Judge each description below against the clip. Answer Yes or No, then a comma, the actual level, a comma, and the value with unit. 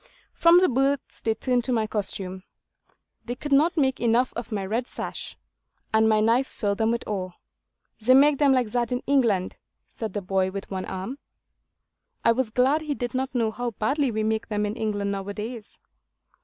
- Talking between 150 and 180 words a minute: No, average, 195 wpm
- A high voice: Yes, high, 230 Hz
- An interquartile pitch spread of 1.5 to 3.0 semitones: No, average, 3.8 semitones